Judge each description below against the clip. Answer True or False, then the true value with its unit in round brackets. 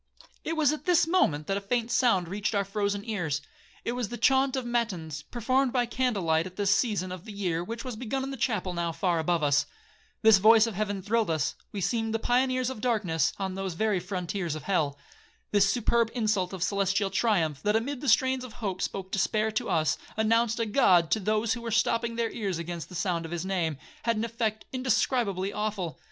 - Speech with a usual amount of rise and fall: True (4.5 semitones)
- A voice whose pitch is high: True (210 Hz)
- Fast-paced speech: True (210 wpm)